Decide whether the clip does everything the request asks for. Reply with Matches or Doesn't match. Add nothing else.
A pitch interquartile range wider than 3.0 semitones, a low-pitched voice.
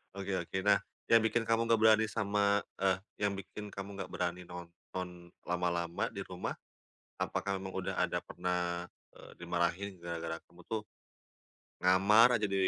Doesn't match